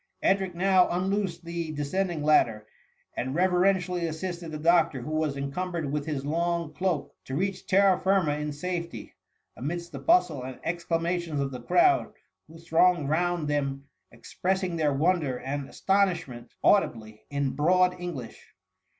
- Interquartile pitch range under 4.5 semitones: Yes, average, 4.0 semitones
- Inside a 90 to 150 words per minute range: Yes, average, 145 wpm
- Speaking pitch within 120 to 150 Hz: No, medium, 170 Hz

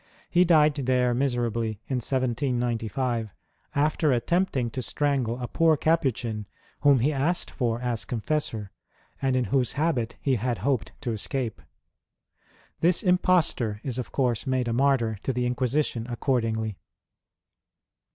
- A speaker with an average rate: No, slow, 130 wpm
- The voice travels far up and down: No, average, 3.4 semitones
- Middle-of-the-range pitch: No, low, 125 Hz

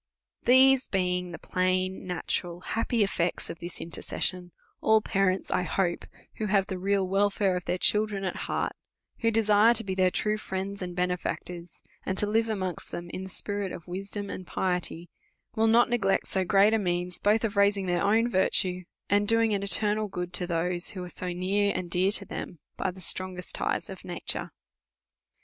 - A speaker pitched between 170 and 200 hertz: Yes, high, 190 Hz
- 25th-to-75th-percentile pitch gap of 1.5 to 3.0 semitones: Yes, narrow, 2.4 semitones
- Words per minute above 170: Yes, average, 190 wpm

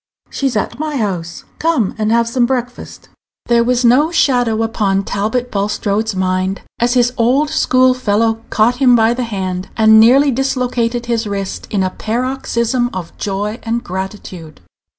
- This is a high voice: Yes, high, 230 Hz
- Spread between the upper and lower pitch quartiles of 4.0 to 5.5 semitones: No, average, 3.5 semitones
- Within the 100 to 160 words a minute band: Yes, average, 155 wpm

